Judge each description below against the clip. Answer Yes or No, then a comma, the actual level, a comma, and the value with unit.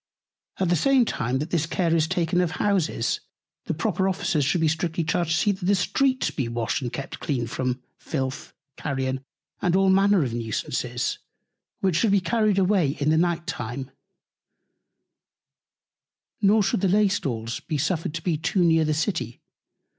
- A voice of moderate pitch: Yes, medium, 165 Hz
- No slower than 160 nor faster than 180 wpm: Yes, average, 170 wpm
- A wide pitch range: Yes, wide, 5.8 semitones